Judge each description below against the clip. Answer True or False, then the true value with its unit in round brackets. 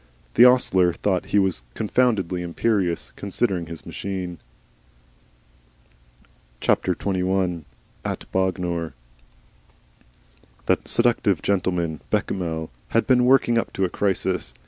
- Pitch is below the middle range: True (95 Hz)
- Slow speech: True (100 wpm)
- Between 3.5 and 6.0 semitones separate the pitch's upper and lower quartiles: False (2.9 semitones)